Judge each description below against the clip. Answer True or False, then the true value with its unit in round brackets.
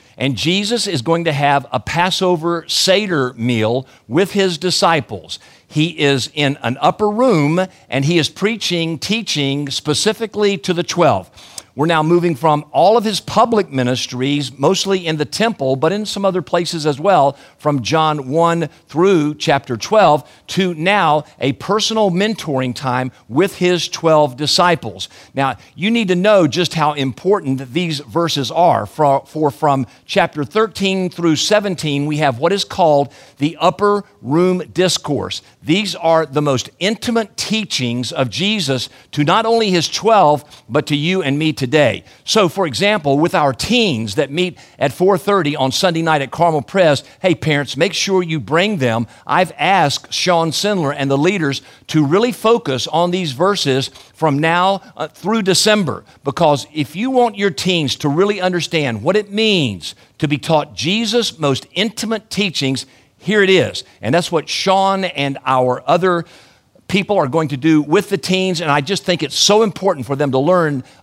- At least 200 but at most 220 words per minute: False (170 wpm)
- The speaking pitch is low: False (160 Hz)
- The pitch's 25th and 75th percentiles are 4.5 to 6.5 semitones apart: True (5.4 semitones)